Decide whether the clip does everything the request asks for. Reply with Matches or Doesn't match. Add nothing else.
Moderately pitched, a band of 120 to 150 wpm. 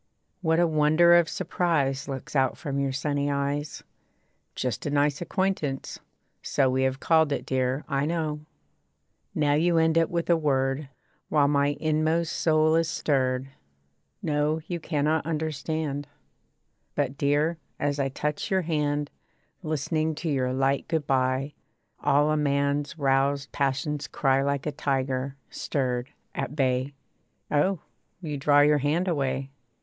Matches